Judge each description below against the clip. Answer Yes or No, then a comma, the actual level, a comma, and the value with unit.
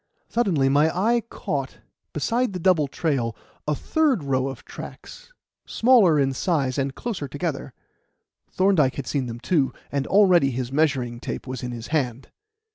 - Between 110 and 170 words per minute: Yes, average, 155 wpm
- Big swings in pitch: Yes, wide, 5.9 semitones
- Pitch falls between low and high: Yes, medium, 145 Hz